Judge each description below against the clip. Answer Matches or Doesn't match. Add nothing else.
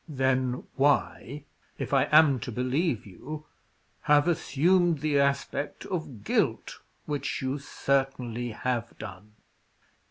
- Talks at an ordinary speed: Doesn't match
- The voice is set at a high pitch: Doesn't match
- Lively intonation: Doesn't match